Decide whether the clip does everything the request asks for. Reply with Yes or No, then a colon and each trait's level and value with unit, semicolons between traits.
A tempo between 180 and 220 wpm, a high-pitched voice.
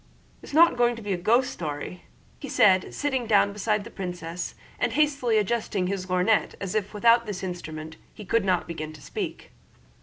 Yes: average, 185 wpm; high, 200 Hz